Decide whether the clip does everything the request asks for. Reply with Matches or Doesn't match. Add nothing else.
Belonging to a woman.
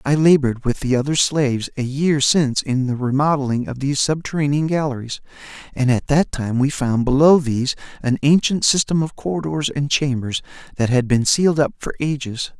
Doesn't match